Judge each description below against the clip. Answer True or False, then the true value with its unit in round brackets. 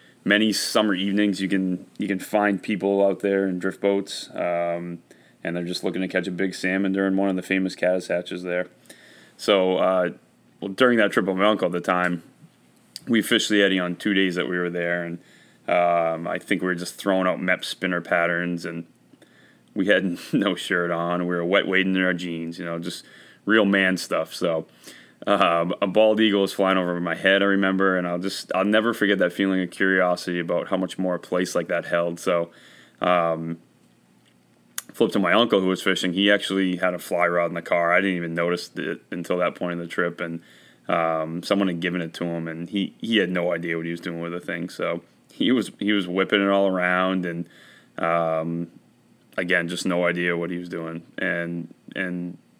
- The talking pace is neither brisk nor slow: False (215 wpm)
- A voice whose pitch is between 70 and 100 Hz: True (90 Hz)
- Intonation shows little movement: True (2.1 semitones)